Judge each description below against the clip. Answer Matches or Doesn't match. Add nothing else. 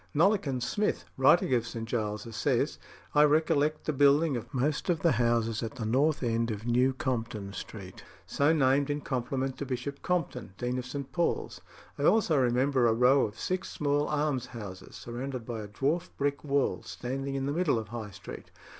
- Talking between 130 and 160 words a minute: Doesn't match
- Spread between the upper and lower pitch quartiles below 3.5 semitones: Doesn't match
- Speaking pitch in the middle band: Doesn't match